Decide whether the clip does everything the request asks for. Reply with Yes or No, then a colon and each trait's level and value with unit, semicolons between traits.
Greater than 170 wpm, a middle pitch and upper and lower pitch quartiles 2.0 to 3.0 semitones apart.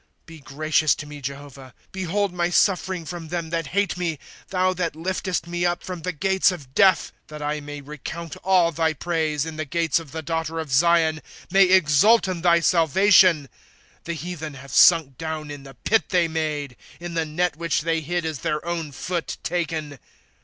Yes: average, 200 wpm; medium, 165 Hz; average, 2.7 semitones